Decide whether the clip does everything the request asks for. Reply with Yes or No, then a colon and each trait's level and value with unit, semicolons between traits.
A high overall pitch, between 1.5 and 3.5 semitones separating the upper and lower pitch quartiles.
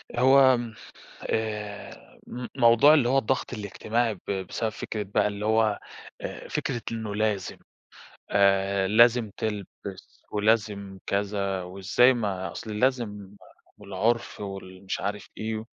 No: low, 105 Hz; average, 2.8 semitones